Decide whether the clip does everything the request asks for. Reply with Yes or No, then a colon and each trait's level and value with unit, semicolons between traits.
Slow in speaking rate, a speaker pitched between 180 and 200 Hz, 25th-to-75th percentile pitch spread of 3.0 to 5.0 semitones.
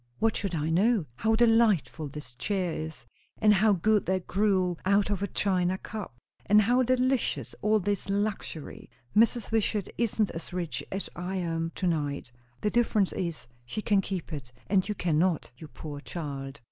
No: average, 170 wpm; high, 190 Hz; average, 4.5 semitones